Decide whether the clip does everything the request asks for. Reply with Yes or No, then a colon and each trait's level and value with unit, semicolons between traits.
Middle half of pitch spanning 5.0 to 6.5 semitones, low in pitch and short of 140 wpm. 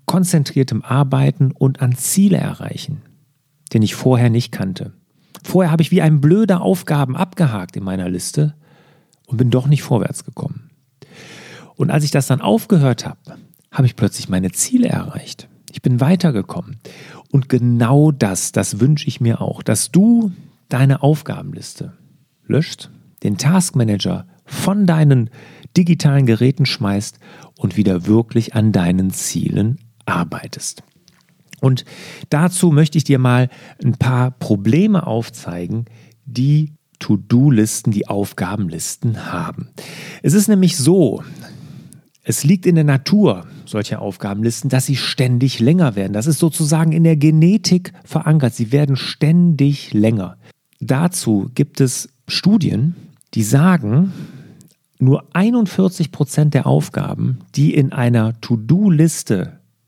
No: wide, 5.5 semitones; medium, 145 Hz; average, 130 wpm